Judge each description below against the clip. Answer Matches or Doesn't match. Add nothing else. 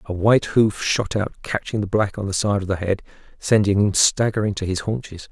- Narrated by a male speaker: Matches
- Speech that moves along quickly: Matches